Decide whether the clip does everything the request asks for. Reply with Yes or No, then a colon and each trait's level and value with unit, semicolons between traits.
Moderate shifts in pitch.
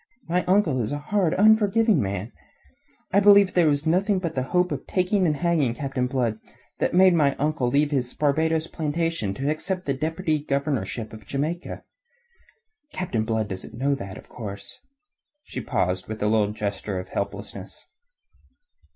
No: wide, 7.8 semitones